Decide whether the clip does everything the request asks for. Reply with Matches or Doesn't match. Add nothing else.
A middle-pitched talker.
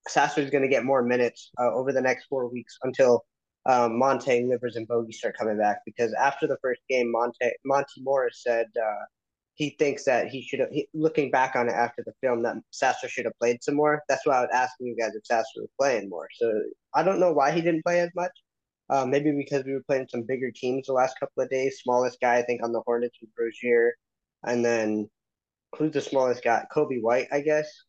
Doesn't match